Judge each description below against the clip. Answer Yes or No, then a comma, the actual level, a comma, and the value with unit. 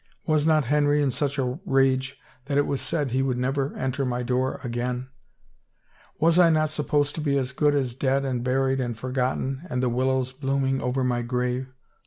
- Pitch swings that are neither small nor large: No, narrow, 2.2 semitones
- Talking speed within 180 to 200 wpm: Yes, average, 190 wpm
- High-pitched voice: No, low, 135 Hz